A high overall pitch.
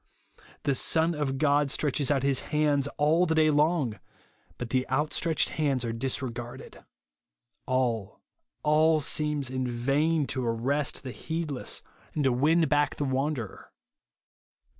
No: medium, 140 Hz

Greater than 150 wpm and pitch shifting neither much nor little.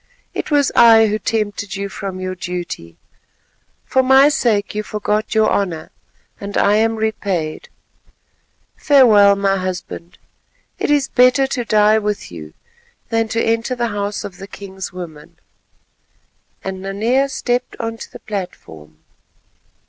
No: average, 140 wpm; average, 3.3 semitones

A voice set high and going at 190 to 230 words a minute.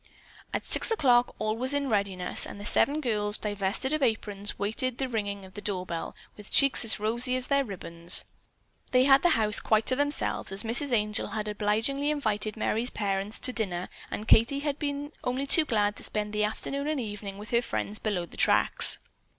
Yes: high, 220 Hz; average, 200 wpm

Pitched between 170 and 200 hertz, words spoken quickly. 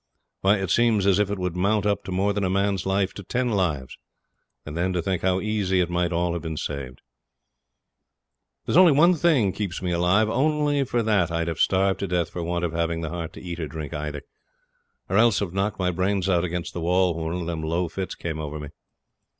No: very low, 90 Hz; fast, 230 wpm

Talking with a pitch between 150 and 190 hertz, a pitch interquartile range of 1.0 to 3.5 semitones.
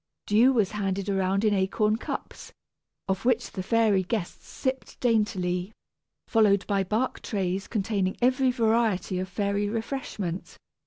No: high, 205 Hz; average, 3.1 semitones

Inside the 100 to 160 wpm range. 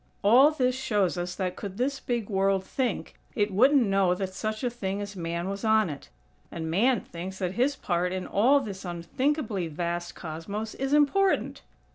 No: average, 180 wpm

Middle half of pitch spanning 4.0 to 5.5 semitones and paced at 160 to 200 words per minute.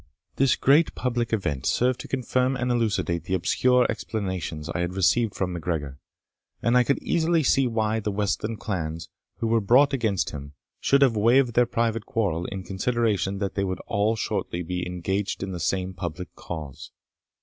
Yes: average, 5.1 semitones; average, 180 wpm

